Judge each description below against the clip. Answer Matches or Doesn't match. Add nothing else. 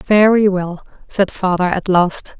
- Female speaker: Matches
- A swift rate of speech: Doesn't match